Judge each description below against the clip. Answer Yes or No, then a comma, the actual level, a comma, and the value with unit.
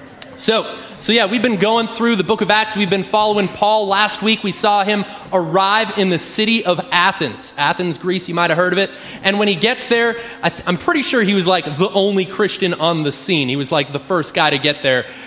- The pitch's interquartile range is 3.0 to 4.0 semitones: Yes, average, 3.5 semitones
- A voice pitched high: Yes, high, 200 Hz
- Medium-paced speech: No, fast, 245 wpm